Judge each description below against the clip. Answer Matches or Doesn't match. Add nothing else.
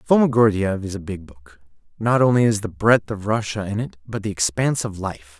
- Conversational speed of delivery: Doesn't match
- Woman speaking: Doesn't match